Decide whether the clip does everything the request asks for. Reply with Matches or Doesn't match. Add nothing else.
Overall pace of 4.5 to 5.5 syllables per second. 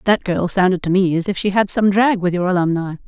Doesn't match